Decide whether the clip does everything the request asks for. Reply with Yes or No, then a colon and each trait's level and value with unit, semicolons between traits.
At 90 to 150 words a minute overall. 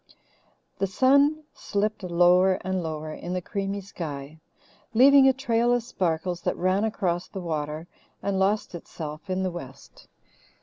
Yes: average, 145 wpm